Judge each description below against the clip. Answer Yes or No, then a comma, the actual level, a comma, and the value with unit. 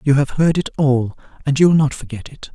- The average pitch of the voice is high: No, medium, 140 Hz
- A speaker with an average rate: No, fast, 235 wpm